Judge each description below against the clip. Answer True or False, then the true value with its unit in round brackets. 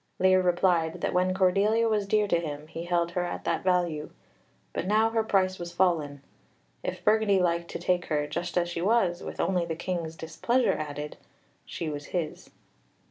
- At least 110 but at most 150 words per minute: False (185 wpm)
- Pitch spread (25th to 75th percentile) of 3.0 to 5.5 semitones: False (2.5 semitones)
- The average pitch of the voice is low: False (175 Hz)